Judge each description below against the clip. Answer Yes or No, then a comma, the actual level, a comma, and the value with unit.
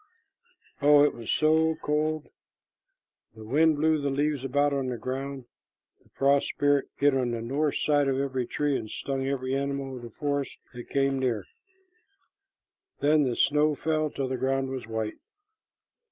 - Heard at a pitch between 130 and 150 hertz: Yes, medium, 140 Hz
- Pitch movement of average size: No, narrow, 2.1 semitones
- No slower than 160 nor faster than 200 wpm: Yes, average, 165 wpm